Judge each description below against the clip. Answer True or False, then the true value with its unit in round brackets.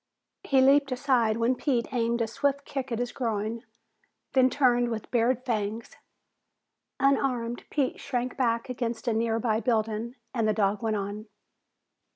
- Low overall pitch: False (235 Hz)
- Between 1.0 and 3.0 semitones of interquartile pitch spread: True (2.4 semitones)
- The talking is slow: False (155 wpm)